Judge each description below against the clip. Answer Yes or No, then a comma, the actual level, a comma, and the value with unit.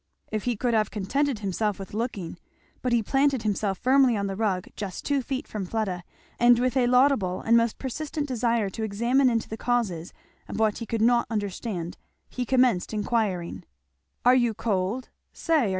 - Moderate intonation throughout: Yes, average, 3.8 semitones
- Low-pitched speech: No, high, 225 Hz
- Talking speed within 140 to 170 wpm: No, average, 180 wpm